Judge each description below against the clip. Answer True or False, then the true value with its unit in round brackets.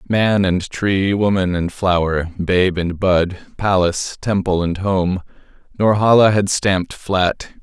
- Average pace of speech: False (125 wpm)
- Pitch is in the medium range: False (95 Hz)